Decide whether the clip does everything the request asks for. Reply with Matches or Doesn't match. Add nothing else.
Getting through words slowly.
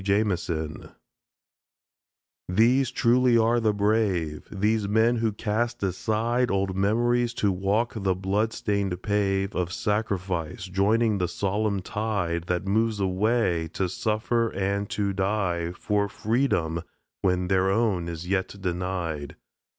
Matches